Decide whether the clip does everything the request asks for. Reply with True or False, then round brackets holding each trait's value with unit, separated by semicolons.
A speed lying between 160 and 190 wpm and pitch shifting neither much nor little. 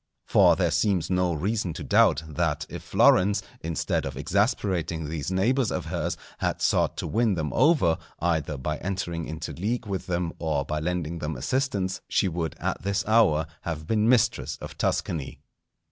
True (170 wpm; 4.3 semitones)